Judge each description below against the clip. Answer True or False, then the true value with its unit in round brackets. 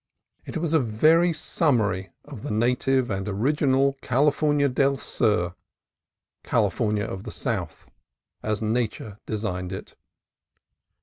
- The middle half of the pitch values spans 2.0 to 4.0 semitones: False (5.1 semitones)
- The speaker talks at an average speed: False (120 wpm)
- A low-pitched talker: True (120 Hz)